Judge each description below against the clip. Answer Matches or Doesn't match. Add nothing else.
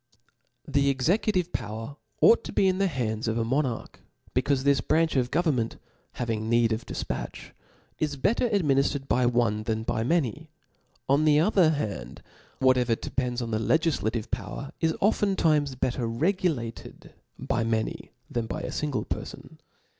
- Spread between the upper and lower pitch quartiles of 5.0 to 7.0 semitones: Matches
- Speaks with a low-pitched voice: Matches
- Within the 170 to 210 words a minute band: Doesn't match